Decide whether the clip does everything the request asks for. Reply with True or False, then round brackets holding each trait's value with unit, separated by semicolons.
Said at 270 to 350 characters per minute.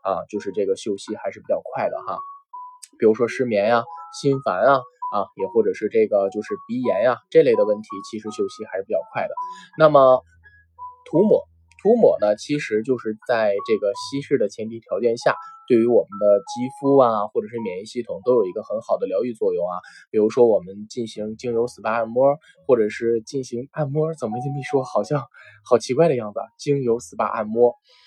True (300 characters per minute)